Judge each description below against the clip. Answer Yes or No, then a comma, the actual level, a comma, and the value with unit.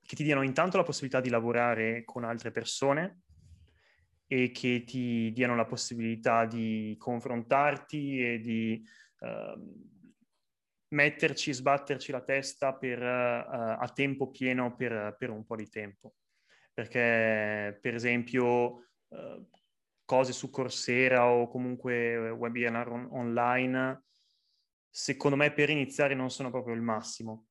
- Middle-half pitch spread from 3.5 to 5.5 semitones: No, average, 2.7 semitones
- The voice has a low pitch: Yes, low, 125 Hz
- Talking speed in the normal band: Yes, average, 125 wpm